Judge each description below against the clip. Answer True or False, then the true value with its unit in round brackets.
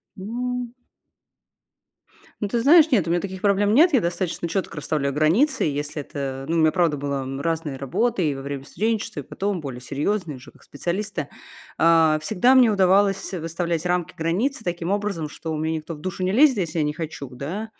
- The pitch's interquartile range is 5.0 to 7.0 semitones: True (5.3 semitones)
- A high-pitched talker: False (170 Hz)